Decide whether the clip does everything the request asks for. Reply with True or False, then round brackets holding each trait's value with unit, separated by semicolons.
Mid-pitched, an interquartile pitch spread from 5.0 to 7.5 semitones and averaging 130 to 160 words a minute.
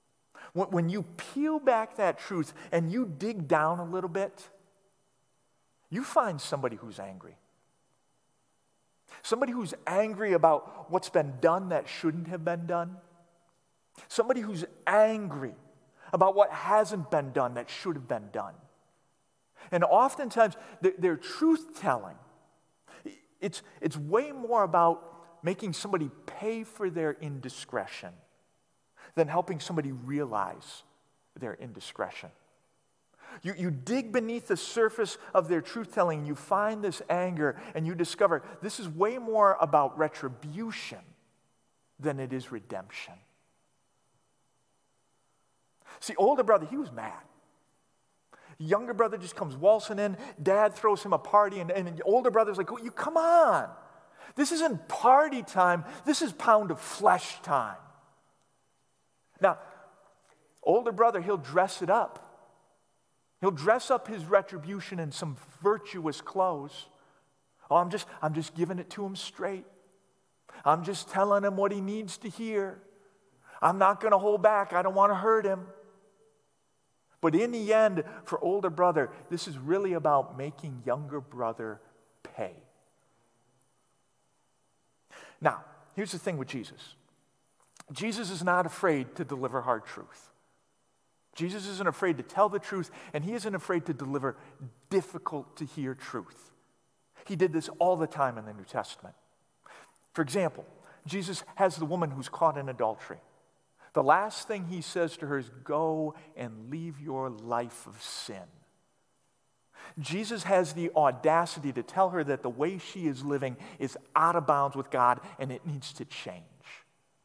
True (180 Hz; 5.4 semitones; 140 wpm)